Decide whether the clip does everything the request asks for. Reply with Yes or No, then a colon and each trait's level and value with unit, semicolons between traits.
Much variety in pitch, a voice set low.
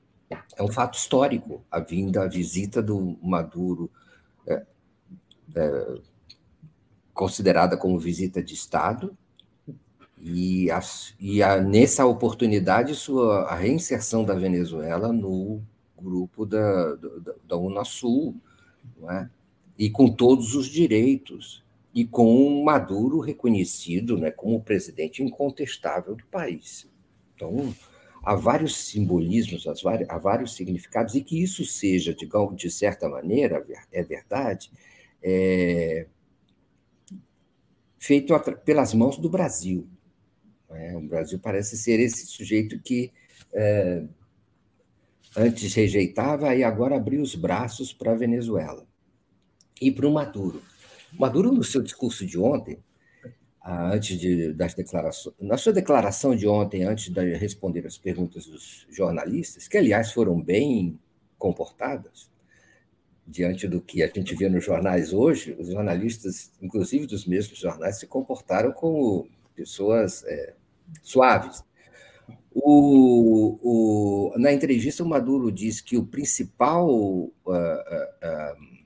Yes: wide, 6.2 semitones; low, 105 Hz